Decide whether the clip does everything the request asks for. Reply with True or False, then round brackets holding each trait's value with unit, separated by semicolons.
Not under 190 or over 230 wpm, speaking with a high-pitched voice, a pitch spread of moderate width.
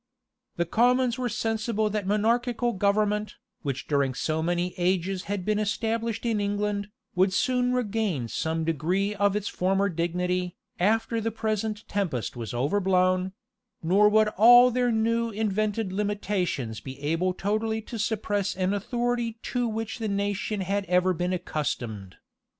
False (145 wpm; 205 Hz; 3.6 semitones)